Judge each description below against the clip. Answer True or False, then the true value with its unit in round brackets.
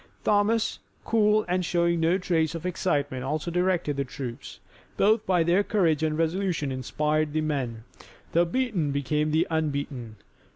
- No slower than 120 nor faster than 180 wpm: True (150 wpm)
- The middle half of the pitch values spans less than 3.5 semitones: False (3.9 semitones)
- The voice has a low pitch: False (160 Hz)